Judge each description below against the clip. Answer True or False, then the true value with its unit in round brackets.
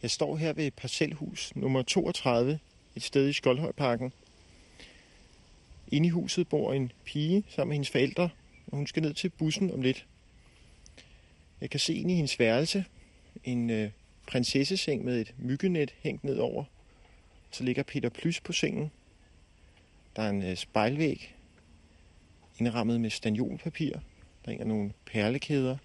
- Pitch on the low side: True (130 Hz)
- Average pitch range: False (6.7 semitones)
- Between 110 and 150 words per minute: True (145 wpm)